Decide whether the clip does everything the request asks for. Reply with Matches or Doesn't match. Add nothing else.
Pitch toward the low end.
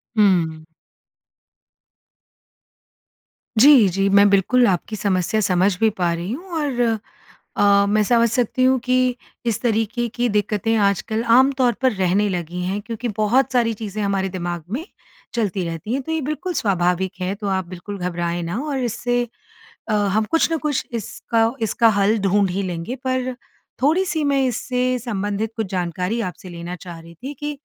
Doesn't match